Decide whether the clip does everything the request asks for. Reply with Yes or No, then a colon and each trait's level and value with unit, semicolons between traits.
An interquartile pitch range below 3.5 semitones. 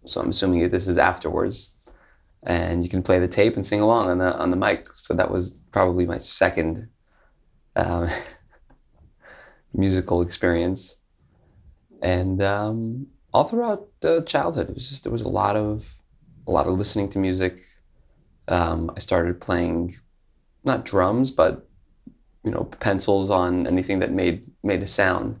Yes: average, 2.9 semitones